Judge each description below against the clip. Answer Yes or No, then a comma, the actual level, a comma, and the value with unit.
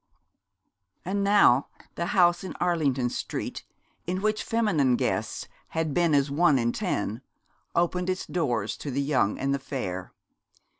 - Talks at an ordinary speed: Yes, average, 145 wpm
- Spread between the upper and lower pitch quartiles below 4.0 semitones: No, wide, 5.4 semitones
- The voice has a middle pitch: Yes, medium, 155 Hz